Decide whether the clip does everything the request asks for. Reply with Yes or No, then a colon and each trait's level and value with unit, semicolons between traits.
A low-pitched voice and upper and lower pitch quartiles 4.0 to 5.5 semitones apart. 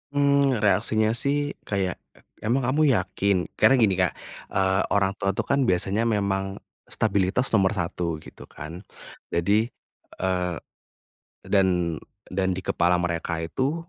Yes: low, 100 Hz; average, 4.3 semitones